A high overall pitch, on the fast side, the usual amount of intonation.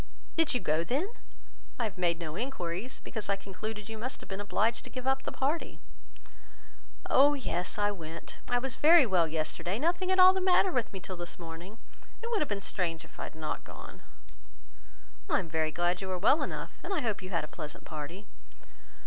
No: high, 200 Hz; fast, 210 wpm; wide, 7.6 semitones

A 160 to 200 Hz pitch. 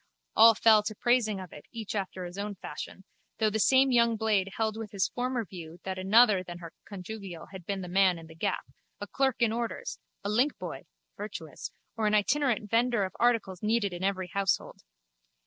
No: high, 210 Hz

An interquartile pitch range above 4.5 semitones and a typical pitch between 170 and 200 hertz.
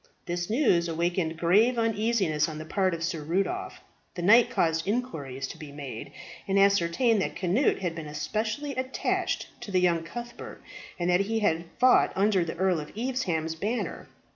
Yes: wide, 5.4 semitones; medium, 185 Hz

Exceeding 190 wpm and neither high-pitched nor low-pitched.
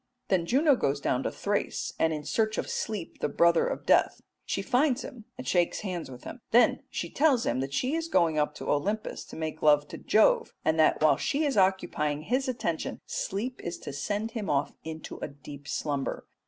Yes: fast, 205 wpm; medium, 175 Hz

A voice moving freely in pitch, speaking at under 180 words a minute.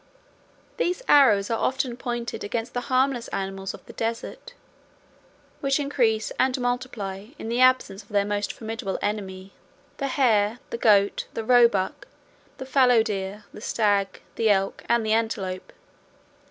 No: average, 3.6 semitones; average, 145 wpm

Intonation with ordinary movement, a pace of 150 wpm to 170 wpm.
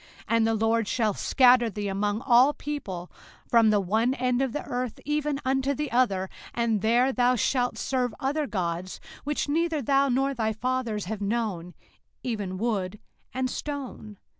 Yes: average, 3.9 semitones; average, 165 wpm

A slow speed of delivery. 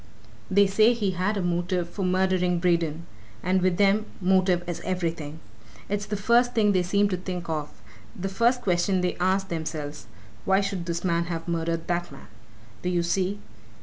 No: average, 175 wpm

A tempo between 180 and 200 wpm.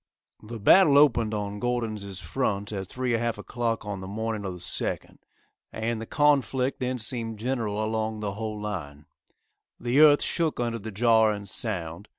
No: average, 165 wpm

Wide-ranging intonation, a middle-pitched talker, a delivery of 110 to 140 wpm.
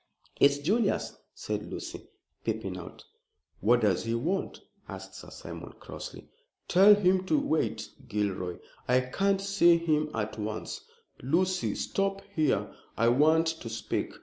Yes: wide, 8.7 semitones; medium, 155 Hz; slow, 135 wpm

